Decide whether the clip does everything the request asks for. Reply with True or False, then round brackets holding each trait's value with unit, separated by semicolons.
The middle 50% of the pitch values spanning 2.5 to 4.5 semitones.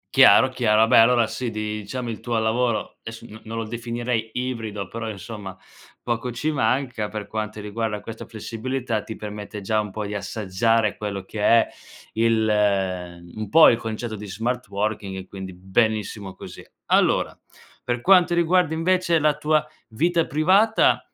True (2.9 semitones)